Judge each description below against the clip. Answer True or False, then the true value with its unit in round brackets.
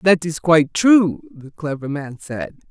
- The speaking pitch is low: False (170 Hz)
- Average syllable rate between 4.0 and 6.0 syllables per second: True (4.1 syllables/s)